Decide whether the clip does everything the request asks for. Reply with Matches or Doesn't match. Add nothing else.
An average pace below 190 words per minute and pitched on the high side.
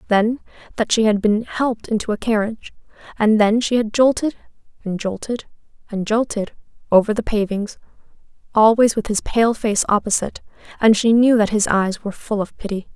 Matches